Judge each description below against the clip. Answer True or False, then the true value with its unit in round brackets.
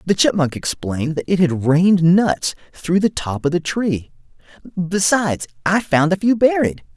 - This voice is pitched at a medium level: True (170 Hz)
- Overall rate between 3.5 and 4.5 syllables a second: False (4.7 syllables/s)